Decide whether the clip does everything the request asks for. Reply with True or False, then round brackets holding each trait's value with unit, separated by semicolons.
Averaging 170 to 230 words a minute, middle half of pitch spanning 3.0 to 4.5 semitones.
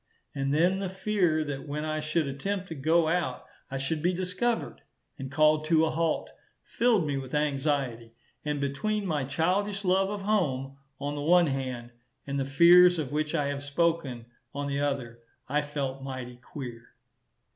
True (175 wpm; 4.1 semitones)